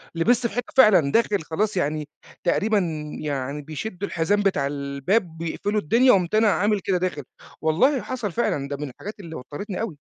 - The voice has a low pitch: No, medium, 185 Hz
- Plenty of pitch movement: Yes, wide, 6.1 semitones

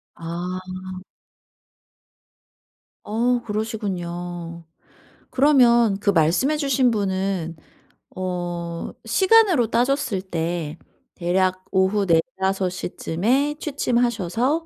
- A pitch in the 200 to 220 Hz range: No, high, 190 Hz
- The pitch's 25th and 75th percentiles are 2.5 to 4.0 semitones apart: No, wide, 5.6 semitones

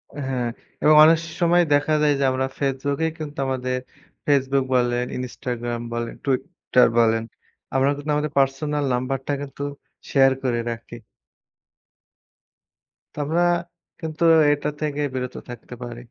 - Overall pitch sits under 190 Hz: Yes, low, 135 Hz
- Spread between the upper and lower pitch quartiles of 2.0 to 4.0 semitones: Yes, average, 2.9 semitones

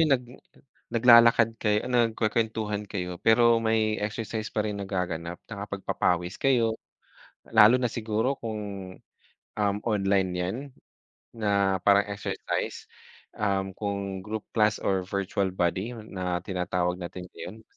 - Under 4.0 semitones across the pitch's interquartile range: Yes, average, 2.8 semitones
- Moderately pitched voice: No, low, 105 Hz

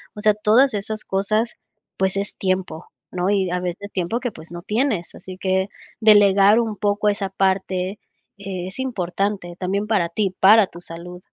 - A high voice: Yes, high, 195 Hz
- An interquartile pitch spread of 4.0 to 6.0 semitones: No, narrow, 2.4 semitones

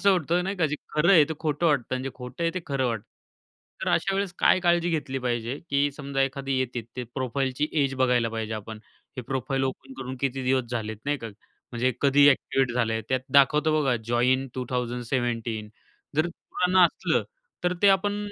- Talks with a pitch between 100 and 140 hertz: Yes, low, 135 Hz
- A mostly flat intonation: No, average, 3.8 semitones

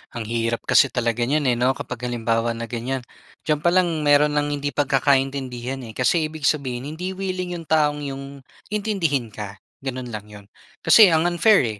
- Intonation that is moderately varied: Yes, average, 4.6 semitones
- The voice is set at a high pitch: No, low, 135 Hz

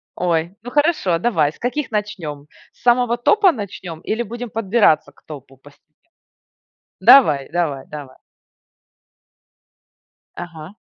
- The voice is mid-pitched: Yes, medium, 180 Hz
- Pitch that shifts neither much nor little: No, wide, 7.7 semitones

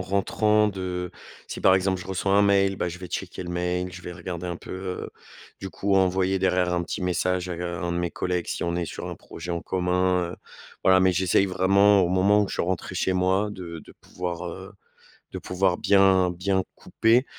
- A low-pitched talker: Yes, very low, 90 Hz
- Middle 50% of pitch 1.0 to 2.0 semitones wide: Yes, narrow, 1.3 semitones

